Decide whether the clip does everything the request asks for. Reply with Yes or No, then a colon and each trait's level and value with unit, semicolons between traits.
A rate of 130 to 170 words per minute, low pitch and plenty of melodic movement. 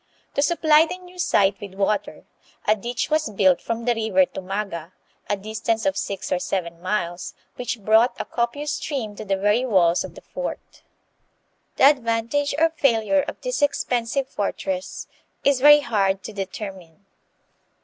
No: average, 160 wpm; high, 220 Hz; wide, 6.4 semitones